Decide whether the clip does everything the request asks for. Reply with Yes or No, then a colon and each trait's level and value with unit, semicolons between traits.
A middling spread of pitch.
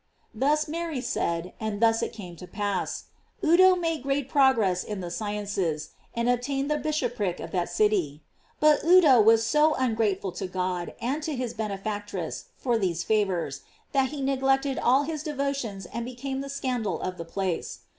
No: wide, 6.3 semitones